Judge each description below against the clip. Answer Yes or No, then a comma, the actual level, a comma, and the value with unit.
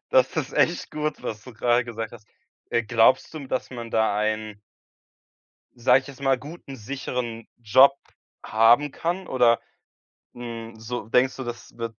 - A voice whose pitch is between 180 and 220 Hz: No, low, 120 Hz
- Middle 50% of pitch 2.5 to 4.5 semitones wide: Yes, average, 2.9 semitones